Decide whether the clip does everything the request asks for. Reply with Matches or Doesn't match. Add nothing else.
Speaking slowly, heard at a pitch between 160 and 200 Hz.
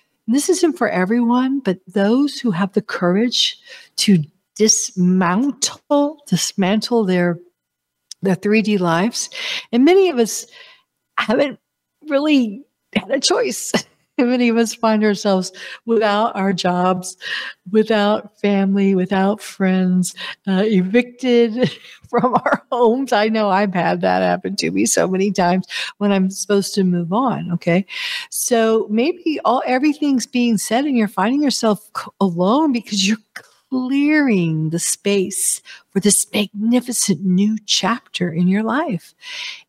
Doesn't match